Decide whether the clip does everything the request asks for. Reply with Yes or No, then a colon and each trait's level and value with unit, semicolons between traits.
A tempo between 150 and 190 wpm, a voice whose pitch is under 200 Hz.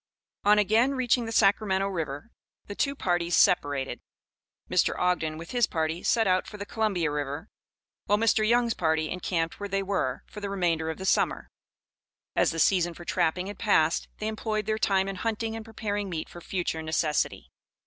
Yes: average, 180 wpm; high, 190 Hz